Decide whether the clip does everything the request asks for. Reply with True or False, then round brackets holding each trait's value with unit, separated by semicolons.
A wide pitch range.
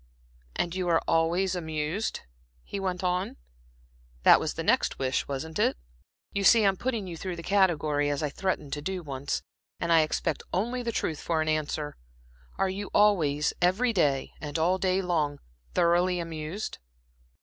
False (3.8 semitones)